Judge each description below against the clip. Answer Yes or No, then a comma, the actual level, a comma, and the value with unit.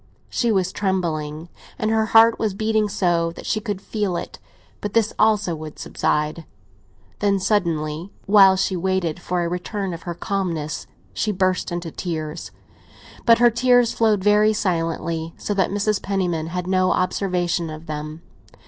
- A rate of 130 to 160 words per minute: Yes, average, 155 wpm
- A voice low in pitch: No, medium, 185 Hz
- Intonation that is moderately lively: Yes, average, 3.7 semitones